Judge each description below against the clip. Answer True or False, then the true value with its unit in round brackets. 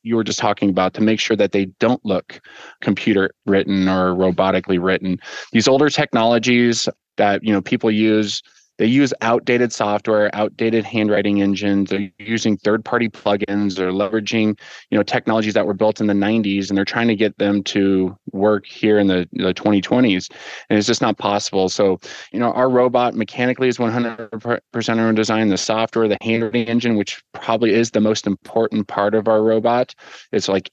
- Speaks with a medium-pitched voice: False (110 Hz)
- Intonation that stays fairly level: True (2.3 semitones)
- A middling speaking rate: True (180 wpm)